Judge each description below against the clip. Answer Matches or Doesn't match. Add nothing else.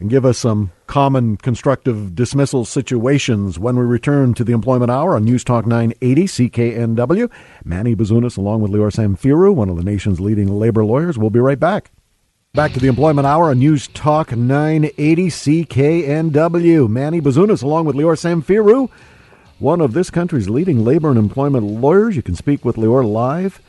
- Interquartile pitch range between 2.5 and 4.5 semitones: Doesn't match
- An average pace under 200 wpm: Matches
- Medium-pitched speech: Doesn't match